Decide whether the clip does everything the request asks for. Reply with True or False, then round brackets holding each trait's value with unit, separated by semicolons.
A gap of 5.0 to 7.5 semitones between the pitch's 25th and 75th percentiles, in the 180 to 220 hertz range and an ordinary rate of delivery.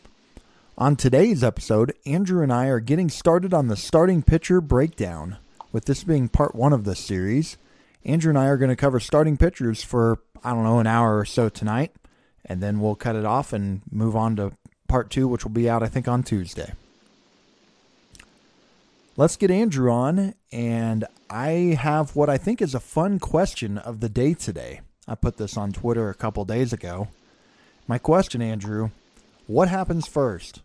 False (5.5 semitones; 125 Hz; 180 wpm)